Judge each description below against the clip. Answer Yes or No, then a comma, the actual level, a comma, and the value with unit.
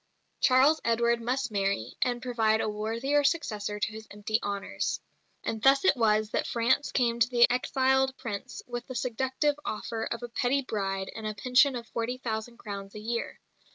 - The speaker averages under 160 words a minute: No, average, 180 wpm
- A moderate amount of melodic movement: Yes, average, 3.1 semitones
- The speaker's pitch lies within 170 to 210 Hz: No, high, 235 Hz